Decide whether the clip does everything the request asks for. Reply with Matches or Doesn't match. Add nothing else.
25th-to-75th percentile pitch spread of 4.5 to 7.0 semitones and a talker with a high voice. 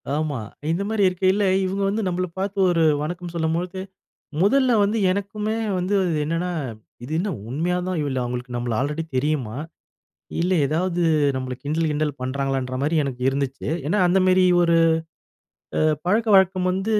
Doesn't match